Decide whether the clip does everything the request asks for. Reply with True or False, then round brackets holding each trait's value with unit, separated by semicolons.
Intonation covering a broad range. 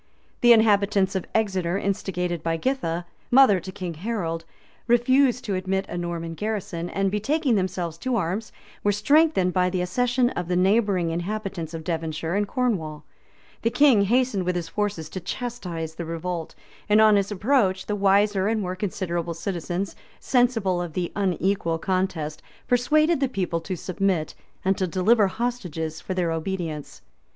False (4.1 semitones)